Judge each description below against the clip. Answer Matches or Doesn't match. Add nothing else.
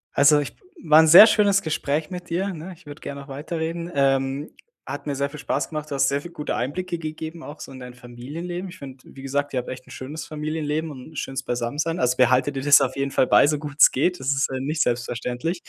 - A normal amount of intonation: Matches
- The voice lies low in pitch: Doesn't match